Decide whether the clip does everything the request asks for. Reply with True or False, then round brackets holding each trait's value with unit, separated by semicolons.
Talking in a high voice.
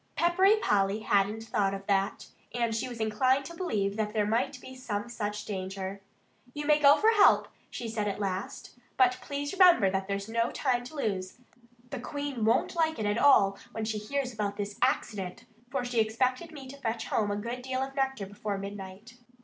True (225 Hz)